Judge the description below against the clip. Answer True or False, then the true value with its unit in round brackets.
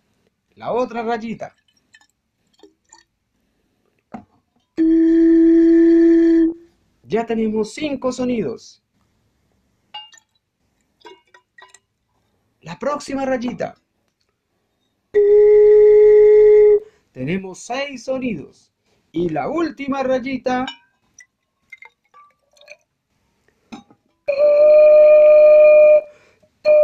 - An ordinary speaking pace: False (40 wpm)